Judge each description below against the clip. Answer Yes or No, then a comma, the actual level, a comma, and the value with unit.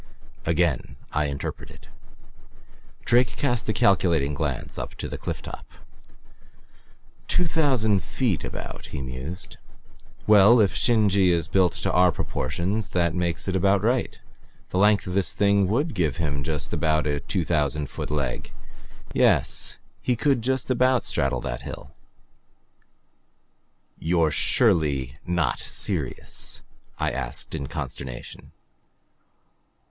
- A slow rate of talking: Yes, slow, 130 wpm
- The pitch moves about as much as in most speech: No, wide, 6.1 semitones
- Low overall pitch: Yes, very low, 90 Hz